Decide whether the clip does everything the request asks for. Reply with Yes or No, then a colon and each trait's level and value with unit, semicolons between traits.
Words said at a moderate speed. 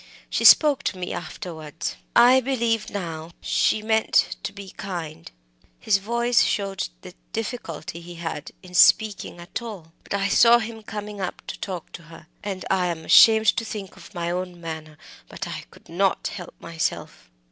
Yes: average, 170 wpm